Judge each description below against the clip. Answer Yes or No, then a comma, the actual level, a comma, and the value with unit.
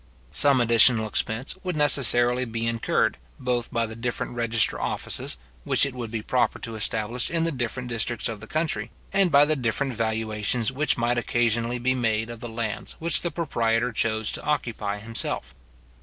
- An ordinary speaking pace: Yes, average, 175 wpm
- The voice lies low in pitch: Yes, low, 120 Hz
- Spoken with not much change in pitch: Yes, narrow, 2.3 semitones